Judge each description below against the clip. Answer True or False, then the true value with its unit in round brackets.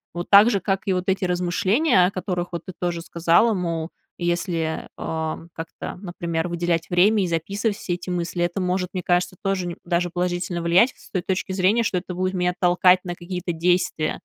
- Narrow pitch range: True (1.4 semitones)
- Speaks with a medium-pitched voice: True (180 Hz)